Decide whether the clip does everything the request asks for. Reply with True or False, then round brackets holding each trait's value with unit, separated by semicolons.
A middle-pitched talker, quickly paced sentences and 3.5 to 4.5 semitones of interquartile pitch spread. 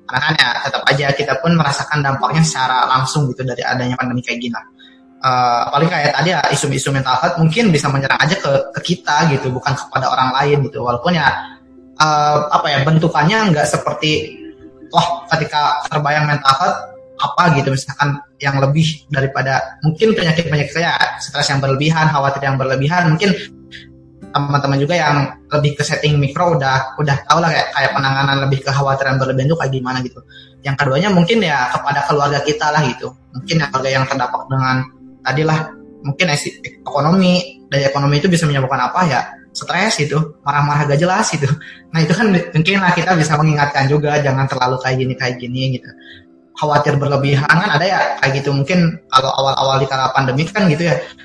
False (145 Hz; 185 wpm; 3.0 semitones)